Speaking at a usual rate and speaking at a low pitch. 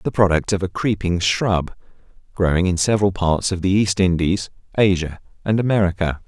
Yes: average, 165 wpm; very low, 95 Hz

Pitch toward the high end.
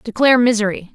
Yes: high, 230 Hz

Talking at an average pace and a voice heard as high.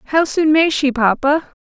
Yes: average, 185 wpm; very high, 290 Hz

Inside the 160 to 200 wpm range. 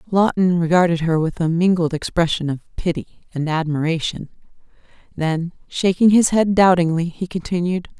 No: slow, 135 wpm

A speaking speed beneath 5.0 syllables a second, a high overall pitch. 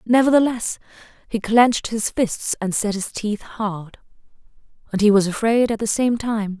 Yes: 4.6 syllables/s; high, 215 Hz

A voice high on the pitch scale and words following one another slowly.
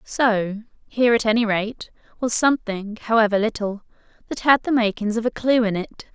No: high, 220 Hz; average, 165 wpm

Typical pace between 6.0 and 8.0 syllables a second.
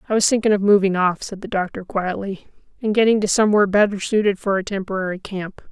Yes: 6.4 syllables/s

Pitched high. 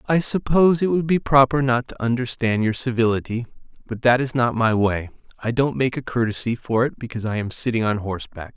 No: low, 120 Hz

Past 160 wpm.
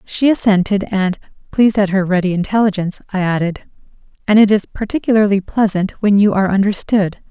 No: average, 155 wpm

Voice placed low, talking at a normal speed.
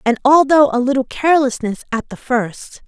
No: very high, 260 Hz; average, 190 wpm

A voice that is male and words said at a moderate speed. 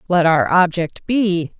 No: female; average, 150 wpm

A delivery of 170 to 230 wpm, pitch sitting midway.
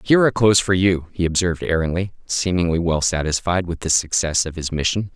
No: average, 200 wpm; very low, 90 Hz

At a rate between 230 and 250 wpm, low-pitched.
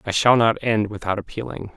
No: fast, 205 wpm; low, 110 Hz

